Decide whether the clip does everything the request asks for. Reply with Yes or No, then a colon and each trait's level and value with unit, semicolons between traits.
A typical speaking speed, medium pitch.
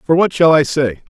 No: fast, 260 wpm; medium, 150 Hz